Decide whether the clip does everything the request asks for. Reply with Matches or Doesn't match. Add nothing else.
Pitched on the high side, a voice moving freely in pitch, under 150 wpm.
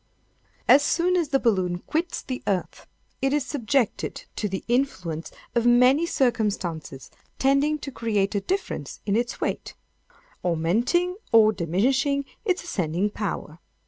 Matches